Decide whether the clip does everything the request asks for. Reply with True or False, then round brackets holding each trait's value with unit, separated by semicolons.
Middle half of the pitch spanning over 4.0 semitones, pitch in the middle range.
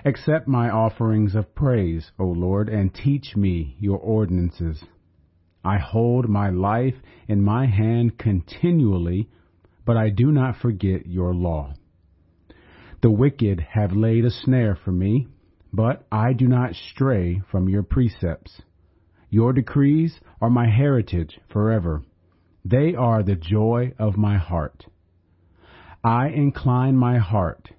False (5.3 semitones; 105 Hz)